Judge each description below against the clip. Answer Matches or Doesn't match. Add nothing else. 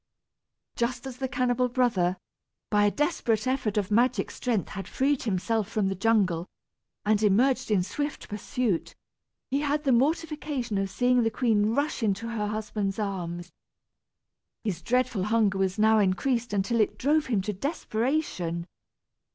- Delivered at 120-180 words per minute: Matches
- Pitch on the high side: Matches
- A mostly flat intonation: Doesn't match